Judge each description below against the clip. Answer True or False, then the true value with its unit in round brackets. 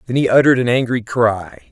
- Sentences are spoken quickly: True (210 wpm)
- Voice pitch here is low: True (115 Hz)